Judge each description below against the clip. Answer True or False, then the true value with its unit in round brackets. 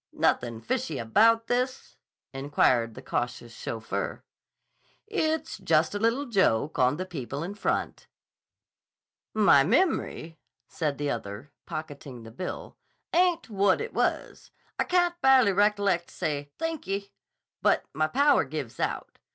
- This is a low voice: False (185 Hz)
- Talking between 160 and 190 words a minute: False (140 wpm)